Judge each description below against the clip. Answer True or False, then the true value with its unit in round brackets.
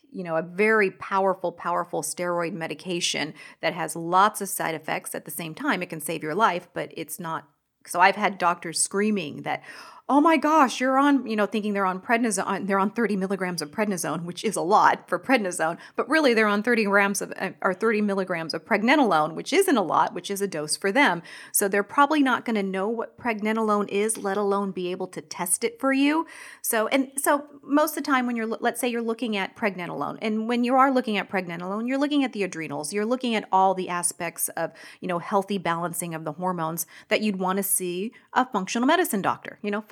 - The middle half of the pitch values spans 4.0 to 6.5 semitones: True (4.9 semitones)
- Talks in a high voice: True (200 Hz)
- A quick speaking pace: True (220 wpm)